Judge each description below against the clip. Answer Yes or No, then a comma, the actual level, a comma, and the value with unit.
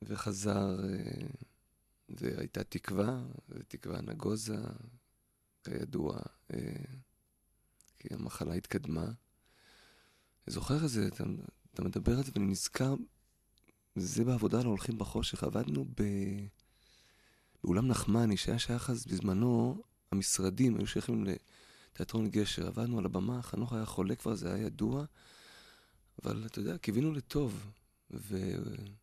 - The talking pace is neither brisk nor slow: No, slow, 110 wpm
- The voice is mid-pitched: No, low, 110 Hz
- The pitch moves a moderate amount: Yes, average, 3.6 semitones